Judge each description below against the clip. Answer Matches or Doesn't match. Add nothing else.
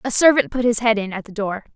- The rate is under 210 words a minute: Doesn't match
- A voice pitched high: Matches